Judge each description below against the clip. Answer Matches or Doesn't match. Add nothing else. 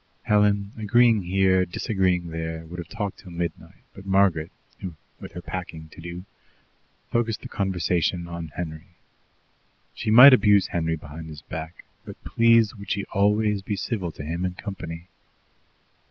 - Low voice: Matches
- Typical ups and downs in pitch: Matches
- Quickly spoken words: Doesn't match